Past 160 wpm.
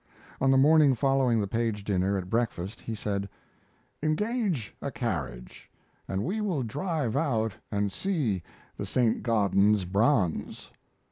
No: slow, 135 wpm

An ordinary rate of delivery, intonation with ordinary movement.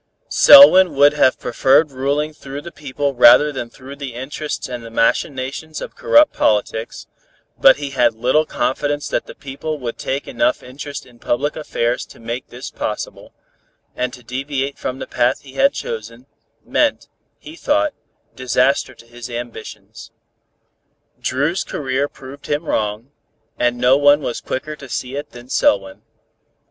Yes: average, 155 wpm; average, 3.1 semitones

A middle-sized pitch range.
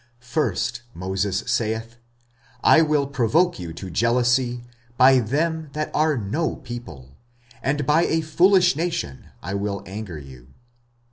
No: wide, 7.5 semitones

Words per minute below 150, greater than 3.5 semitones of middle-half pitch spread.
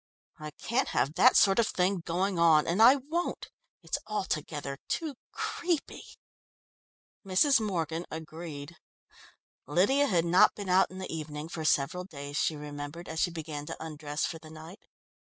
No: average, 155 wpm; average, 4.1 semitones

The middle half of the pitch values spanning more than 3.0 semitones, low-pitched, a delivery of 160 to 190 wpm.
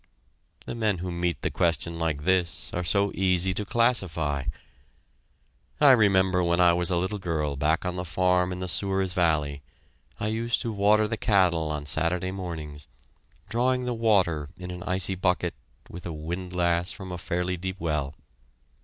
No: narrow, 2.4 semitones; very low, 90 Hz; average, 170 wpm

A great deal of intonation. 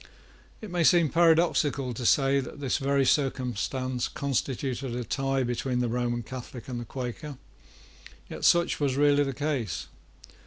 No: average, 2.7 semitones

